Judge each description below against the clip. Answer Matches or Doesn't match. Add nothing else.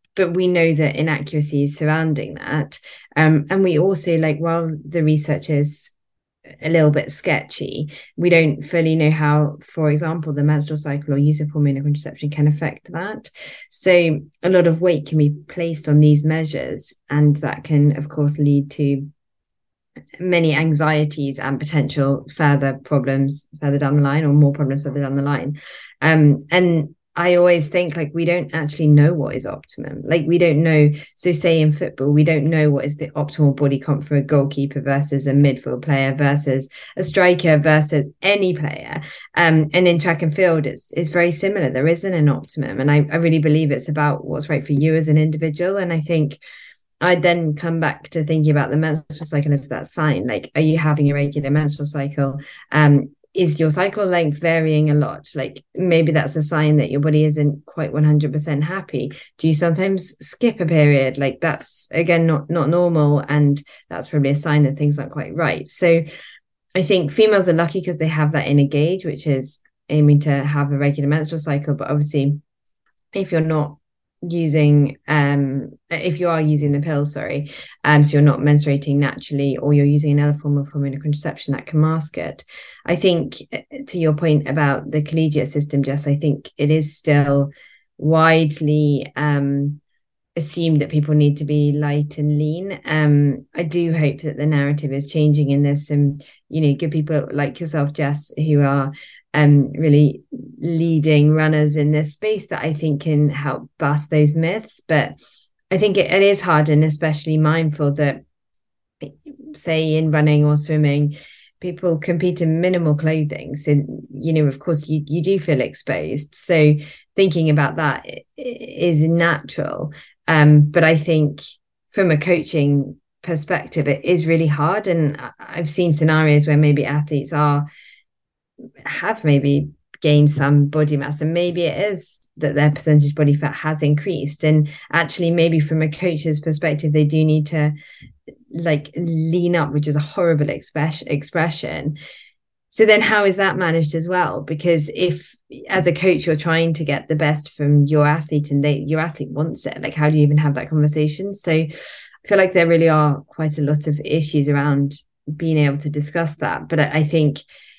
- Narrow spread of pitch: Matches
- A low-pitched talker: Doesn't match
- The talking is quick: Doesn't match